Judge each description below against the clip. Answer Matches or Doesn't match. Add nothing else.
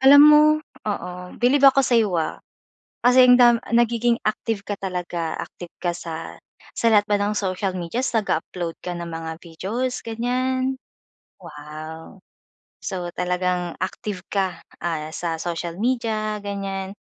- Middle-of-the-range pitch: Doesn't match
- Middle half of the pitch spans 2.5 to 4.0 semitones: Doesn't match